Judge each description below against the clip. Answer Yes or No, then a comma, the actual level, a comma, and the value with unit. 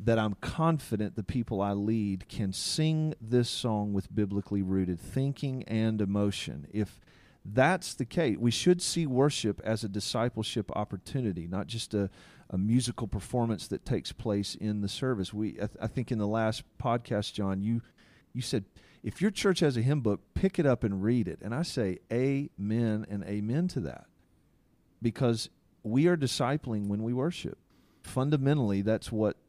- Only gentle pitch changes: No, average, 4.0 semitones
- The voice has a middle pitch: No, low, 110 Hz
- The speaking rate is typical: Yes, average, 175 wpm